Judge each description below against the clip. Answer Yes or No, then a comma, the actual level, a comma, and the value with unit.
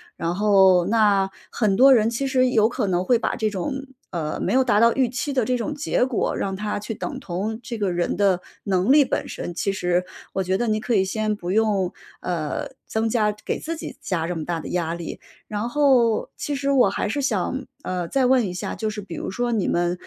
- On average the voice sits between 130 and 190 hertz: No, high, 215 Hz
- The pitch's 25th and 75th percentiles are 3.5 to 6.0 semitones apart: Yes, average, 4.9 semitones